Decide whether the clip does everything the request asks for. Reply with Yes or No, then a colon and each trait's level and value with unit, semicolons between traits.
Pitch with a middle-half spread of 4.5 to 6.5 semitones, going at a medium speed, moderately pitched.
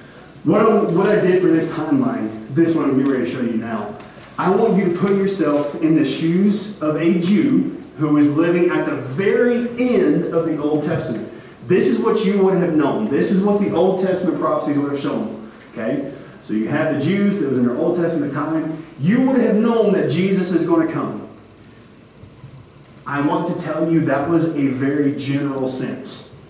No: average, 5.0 semitones; fast, 210 wpm; medium, 160 Hz